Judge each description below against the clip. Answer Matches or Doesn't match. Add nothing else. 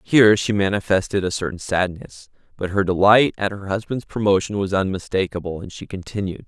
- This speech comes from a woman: Doesn't match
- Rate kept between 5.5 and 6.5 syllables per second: Matches